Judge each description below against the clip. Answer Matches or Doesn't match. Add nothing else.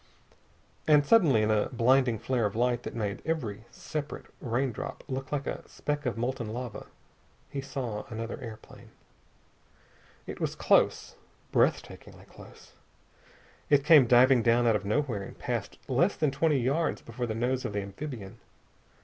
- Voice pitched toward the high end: Doesn't match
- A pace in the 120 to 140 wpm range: Doesn't match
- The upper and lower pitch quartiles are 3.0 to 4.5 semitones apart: Matches